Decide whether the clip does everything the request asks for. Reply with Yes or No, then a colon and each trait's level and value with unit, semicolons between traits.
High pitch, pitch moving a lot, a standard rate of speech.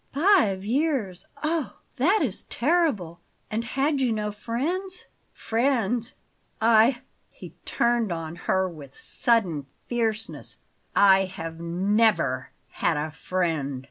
No: high, 220 Hz; wide, 6.5 semitones; slow, 110 wpm